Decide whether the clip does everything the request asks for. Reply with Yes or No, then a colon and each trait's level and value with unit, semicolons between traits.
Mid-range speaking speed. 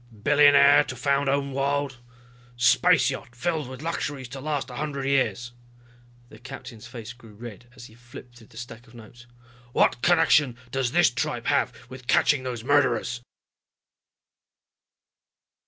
Yes: average, 145 wpm